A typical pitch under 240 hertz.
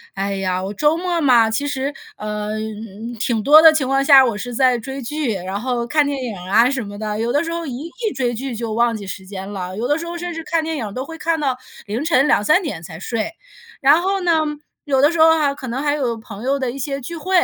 No: very high, 255 Hz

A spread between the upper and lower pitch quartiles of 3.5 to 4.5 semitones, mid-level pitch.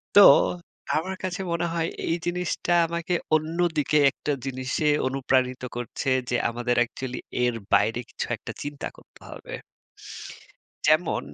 No: average, 5.0 semitones; medium, 150 Hz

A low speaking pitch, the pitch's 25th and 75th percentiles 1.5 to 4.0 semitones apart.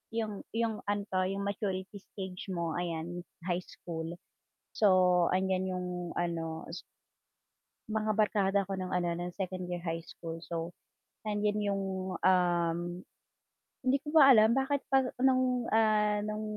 No: high, 190 Hz; average, 3.2 semitones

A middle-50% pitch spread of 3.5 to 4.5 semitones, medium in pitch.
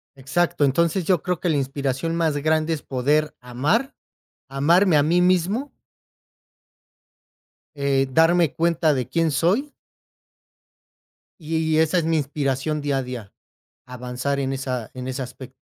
Yes: average, 3.9 semitones; medium, 150 Hz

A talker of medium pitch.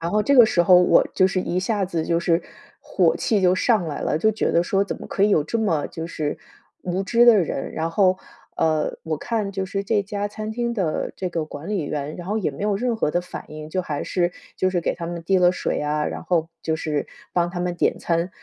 Yes: medium, 180 Hz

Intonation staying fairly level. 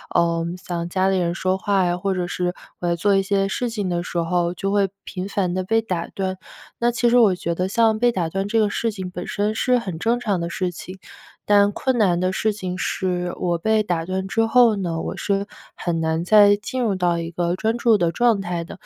No: average, 3.1 semitones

